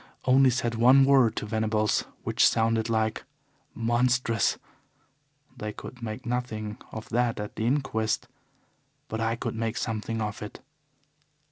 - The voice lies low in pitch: Yes, low, 115 Hz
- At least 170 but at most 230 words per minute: No, slow, 135 wpm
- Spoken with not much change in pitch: Yes, narrow, 1.9 semitones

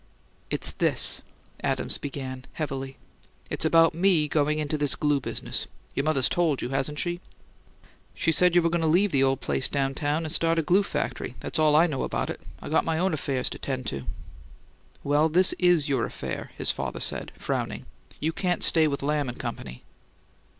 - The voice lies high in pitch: No, medium, 150 Hz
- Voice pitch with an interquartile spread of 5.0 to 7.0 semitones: No, average, 3.2 semitones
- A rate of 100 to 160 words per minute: No, average, 190 wpm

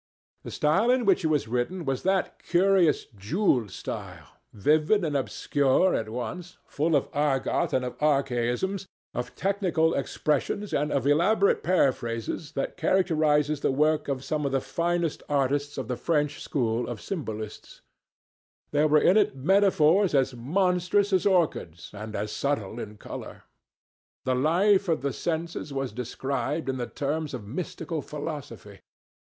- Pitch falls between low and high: Yes, medium, 150 Hz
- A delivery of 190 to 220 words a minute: No, average, 150 wpm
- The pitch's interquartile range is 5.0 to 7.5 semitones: Yes, average, 5.3 semitones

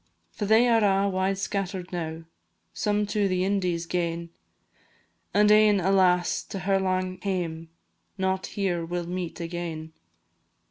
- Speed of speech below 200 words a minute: Yes, average, 140 wpm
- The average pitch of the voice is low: No, medium, 185 Hz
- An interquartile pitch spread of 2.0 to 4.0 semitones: Yes, narrow, 2.4 semitones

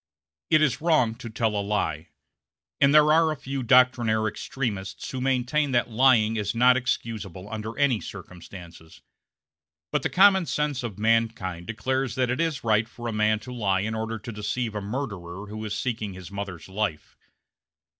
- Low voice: Yes, low, 115 Hz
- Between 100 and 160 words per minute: No, average, 175 wpm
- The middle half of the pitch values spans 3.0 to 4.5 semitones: Yes, average, 4.1 semitones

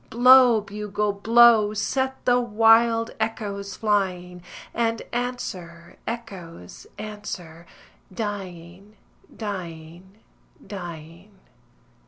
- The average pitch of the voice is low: No, high, 205 Hz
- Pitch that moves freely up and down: No, average, 4.1 semitones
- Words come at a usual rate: No, slow, 75 wpm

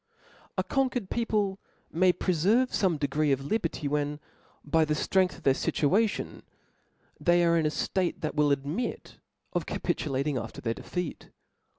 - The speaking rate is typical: Yes, average, 155 wpm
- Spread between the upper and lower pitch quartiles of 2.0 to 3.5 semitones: No, average, 4.8 semitones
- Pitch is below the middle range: No, medium, 160 Hz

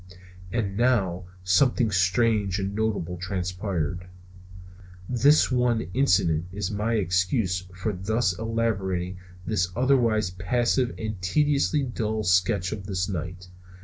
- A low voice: Yes, low, 100 Hz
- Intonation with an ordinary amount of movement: Yes, average, 4.1 semitones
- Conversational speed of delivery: No, slow, 115 wpm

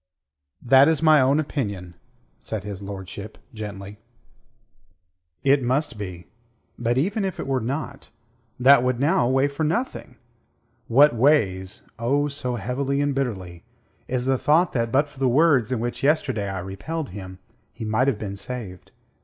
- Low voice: Yes, low, 125 Hz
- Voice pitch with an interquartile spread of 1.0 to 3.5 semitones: No, wide, 5.4 semitones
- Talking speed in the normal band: Yes, average, 155 wpm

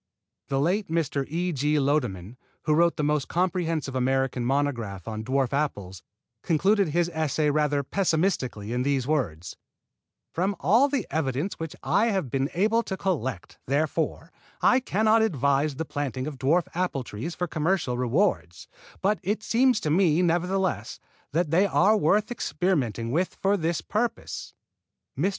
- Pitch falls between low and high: Yes, medium, 155 Hz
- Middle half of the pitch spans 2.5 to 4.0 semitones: No, wide, 5.6 semitones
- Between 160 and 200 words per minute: No, average, 150 wpm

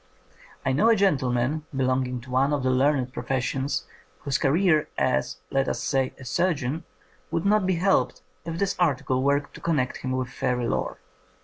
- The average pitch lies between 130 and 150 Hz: Yes, low, 135 Hz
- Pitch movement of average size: Yes, average, 4.2 semitones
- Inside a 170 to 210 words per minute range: Yes, average, 175 wpm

